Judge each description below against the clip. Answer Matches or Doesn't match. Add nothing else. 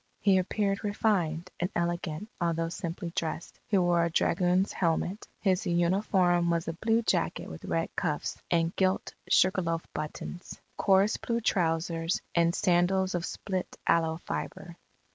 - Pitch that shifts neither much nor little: Doesn't match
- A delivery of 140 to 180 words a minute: Matches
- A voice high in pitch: Doesn't match